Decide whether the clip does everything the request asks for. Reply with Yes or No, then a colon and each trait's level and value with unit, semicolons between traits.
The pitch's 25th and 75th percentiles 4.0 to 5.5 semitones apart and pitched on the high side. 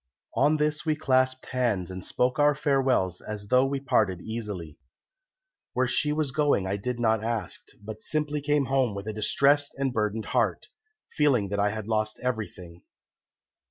No: average, 5.2 semitones; low, 120 Hz